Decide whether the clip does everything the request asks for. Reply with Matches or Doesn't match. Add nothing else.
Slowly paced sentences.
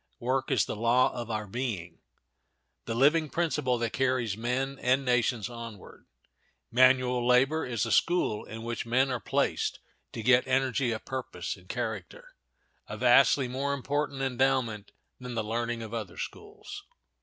Doesn't match